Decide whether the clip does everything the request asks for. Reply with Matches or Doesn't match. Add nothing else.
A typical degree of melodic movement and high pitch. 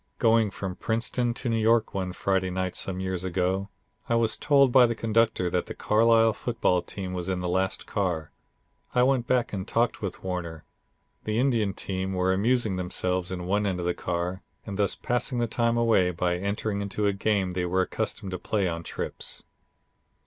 Doesn't match